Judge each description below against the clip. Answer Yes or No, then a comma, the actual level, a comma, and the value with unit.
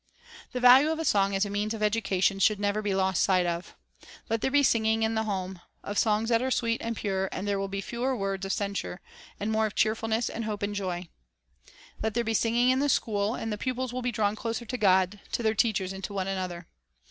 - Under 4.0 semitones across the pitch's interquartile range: Yes, average, 2.8 semitones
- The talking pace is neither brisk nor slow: No, fast, 240 wpm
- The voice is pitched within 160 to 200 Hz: No, high, 210 Hz